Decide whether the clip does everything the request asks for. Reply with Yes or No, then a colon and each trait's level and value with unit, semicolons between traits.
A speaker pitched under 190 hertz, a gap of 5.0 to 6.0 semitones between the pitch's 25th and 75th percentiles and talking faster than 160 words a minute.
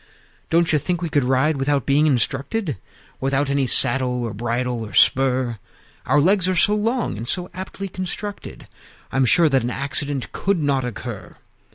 Yes: medium, 140 Hz; average, 5.3 semitones; average, 175 wpm